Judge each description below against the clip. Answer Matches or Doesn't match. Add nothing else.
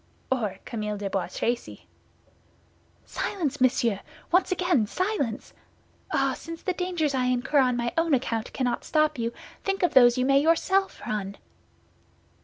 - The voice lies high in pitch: Matches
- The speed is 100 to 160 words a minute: Matches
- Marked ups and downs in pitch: Matches